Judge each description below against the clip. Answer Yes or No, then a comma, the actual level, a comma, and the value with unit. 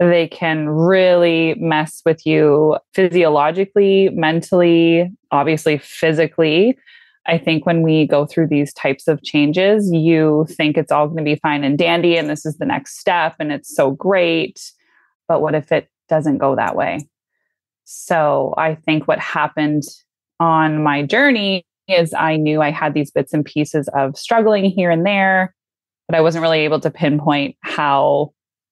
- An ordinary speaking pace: Yes, average, 165 wpm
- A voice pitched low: No, medium, 160 Hz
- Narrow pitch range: Yes, narrow, 2.2 semitones